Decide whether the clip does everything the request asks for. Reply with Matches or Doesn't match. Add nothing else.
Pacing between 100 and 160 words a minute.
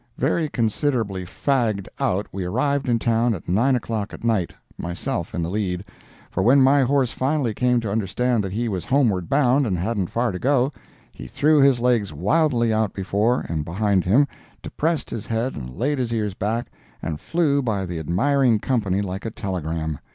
Doesn't match